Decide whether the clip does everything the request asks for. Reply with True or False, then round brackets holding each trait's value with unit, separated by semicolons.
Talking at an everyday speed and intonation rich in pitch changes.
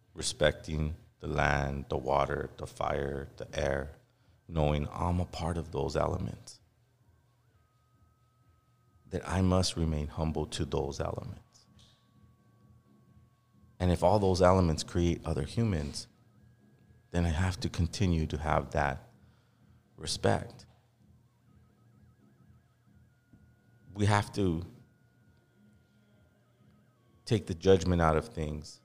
False (105 wpm; 6.3 semitones)